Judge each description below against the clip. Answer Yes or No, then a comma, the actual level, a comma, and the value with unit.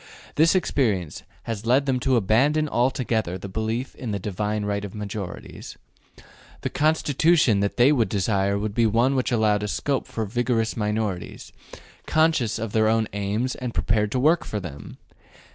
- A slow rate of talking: No, average, 160 wpm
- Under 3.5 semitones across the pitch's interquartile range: No, average, 3.9 semitones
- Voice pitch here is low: Yes, low, 110 Hz